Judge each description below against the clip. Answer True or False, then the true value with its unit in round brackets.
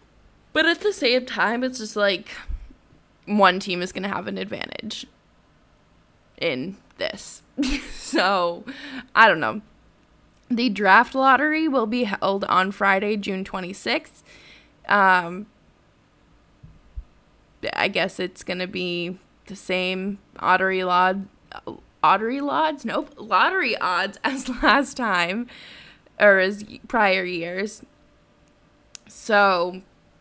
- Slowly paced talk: True (110 wpm)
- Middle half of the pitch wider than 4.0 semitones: True (5.4 semitones)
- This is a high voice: True (205 Hz)